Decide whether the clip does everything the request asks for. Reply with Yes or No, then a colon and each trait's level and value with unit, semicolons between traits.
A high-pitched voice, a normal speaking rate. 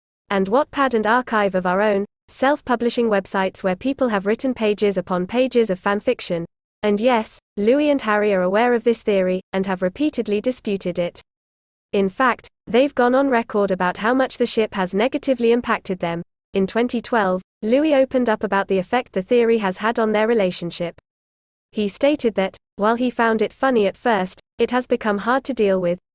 Yes: high, 220 Hz; average, 185 wpm